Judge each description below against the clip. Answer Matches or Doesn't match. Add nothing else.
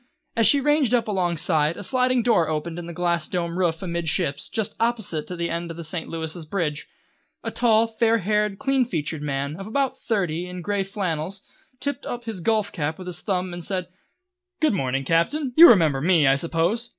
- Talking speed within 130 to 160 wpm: Doesn't match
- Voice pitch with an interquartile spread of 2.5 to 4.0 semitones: Doesn't match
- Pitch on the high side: Doesn't match